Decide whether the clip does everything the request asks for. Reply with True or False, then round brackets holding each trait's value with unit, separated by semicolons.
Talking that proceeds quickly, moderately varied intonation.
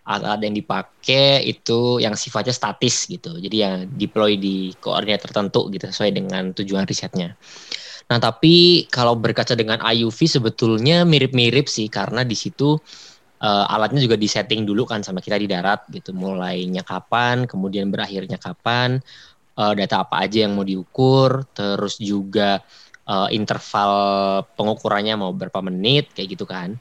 True (145 wpm; 3.8 semitones)